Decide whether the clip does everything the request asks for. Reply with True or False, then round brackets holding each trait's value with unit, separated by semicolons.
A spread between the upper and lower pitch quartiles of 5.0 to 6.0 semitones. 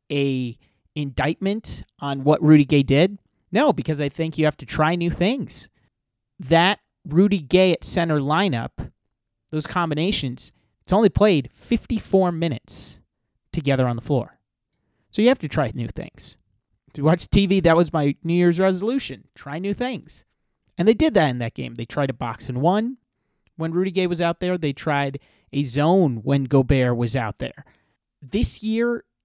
True (5.3 semitones)